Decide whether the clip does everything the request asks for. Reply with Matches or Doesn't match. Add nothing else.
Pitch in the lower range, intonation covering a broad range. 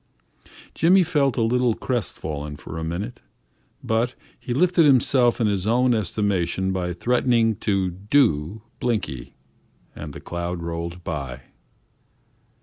Matches